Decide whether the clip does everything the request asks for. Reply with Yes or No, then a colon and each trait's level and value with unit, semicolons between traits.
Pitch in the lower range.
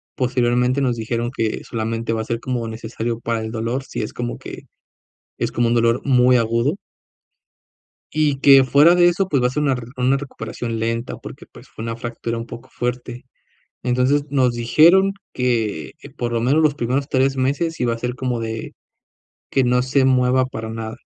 Yes: low, 125 Hz